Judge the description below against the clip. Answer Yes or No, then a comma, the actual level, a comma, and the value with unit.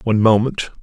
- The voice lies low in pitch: Yes, low, 110 Hz